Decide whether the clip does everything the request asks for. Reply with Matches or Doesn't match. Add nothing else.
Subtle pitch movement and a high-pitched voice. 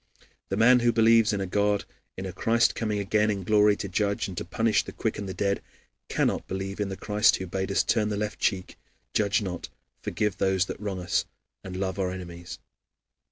Doesn't match